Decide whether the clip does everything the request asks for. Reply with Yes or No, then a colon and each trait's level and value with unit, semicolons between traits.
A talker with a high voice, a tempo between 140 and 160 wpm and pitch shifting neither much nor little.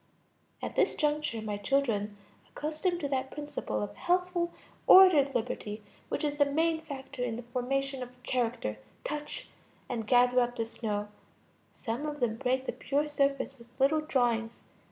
Yes: very high, 265 Hz; average, 155 wpm; average, 4.1 semitones